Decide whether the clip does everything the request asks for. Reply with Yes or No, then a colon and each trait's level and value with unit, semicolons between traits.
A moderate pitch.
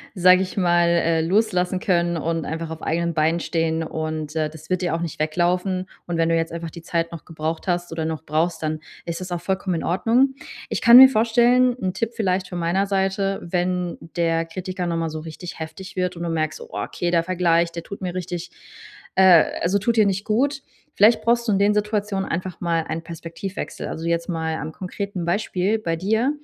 Yes: medium, 175 Hz